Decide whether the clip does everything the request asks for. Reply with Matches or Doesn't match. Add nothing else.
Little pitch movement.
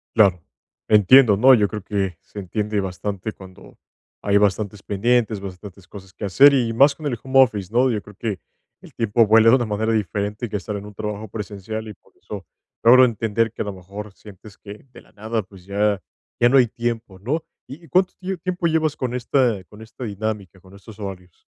Doesn't match